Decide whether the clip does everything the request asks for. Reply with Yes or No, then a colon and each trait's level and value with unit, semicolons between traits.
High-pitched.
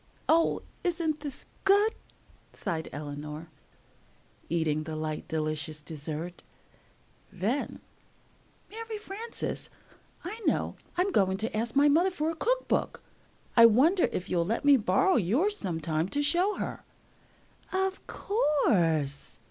Yes: high, 230 Hz